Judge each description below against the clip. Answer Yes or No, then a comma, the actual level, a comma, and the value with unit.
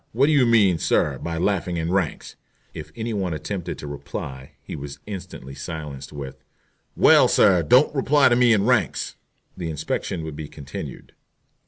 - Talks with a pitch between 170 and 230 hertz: No, very low, 85 Hz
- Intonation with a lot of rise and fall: Yes, wide, 7.1 semitones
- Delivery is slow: No, average, 170 wpm